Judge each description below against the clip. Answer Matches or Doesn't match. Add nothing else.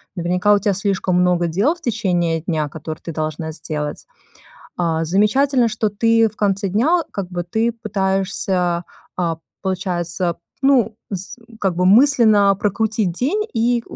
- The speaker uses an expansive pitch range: Doesn't match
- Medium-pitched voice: Doesn't match